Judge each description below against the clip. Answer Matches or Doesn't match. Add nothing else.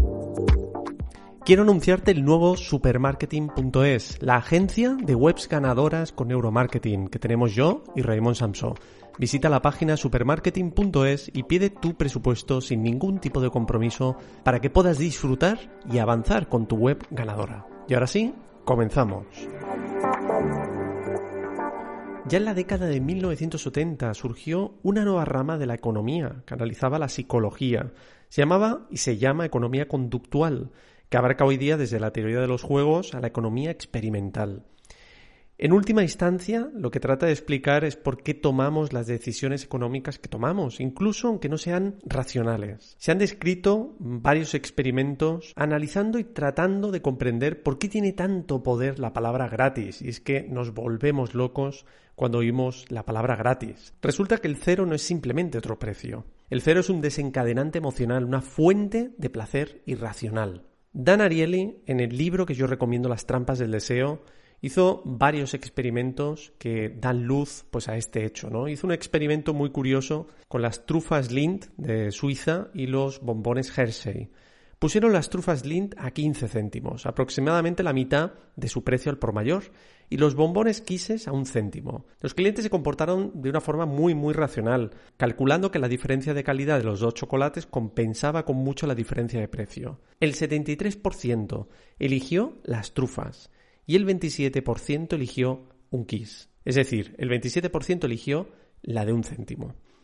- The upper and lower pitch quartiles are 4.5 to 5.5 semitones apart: Matches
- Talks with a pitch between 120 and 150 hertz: Matches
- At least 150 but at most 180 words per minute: Matches